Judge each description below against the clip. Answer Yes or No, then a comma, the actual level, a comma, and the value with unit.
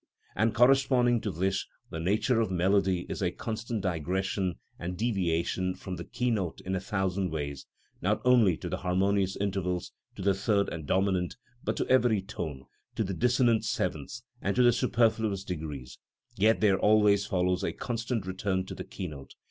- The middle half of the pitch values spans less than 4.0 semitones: Yes, average, 3.6 semitones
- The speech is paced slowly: No, average, 175 wpm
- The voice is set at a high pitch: No, very low, 95 Hz